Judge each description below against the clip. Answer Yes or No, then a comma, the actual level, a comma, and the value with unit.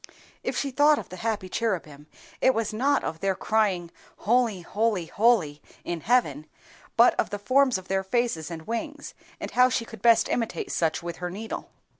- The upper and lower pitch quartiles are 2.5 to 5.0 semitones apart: No, wide, 5.5 semitones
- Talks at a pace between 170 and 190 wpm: Yes, average, 185 wpm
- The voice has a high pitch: Yes, high, 215 Hz